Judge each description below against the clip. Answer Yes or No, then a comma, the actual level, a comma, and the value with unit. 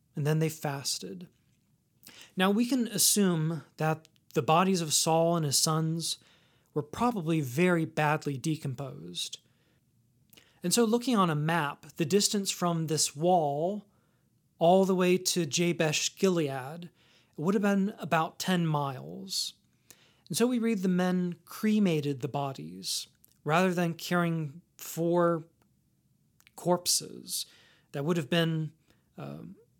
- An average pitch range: Yes, average, 3.4 semitones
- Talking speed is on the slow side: Yes, slow, 125 wpm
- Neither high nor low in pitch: Yes, medium, 165 Hz